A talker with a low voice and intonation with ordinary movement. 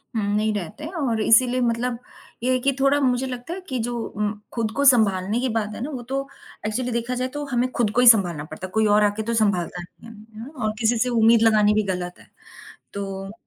No: high, 230 Hz; average, 3.1 semitones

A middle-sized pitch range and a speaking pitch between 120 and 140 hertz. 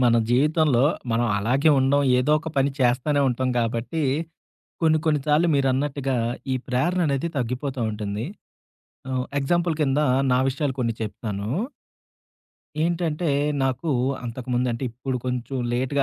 Yes: average, 3.3 semitones; low, 135 Hz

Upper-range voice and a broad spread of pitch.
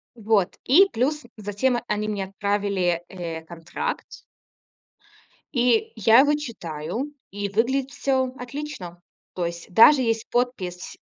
Yes: high, 220 Hz; wide, 6.1 semitones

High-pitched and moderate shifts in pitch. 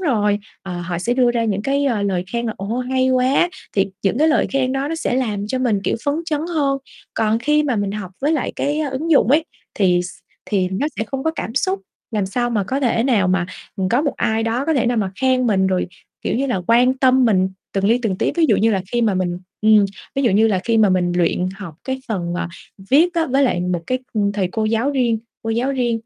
Yes: high, 230 Hz; average, 5.0 semitones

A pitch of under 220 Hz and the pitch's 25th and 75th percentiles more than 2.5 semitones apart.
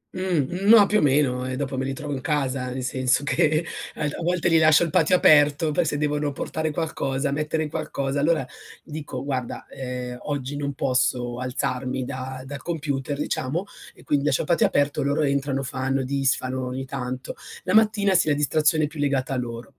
Yes: medium, 140 Hz; average, 2.9 semitones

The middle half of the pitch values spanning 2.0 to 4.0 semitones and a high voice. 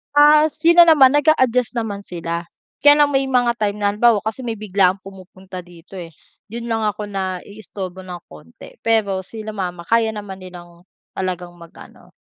No: average, 4.4 semitones; high, 205 Hz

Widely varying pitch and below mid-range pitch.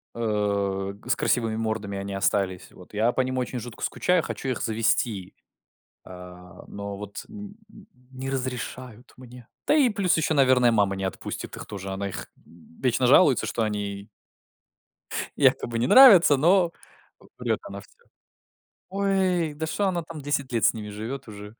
Yes: wide, 6.2 semitones; low, 120 Hz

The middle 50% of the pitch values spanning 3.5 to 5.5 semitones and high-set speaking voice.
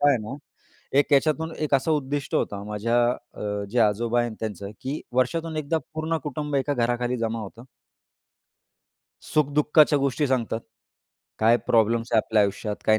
No: average, 4.6 semitones; low, 125 Hz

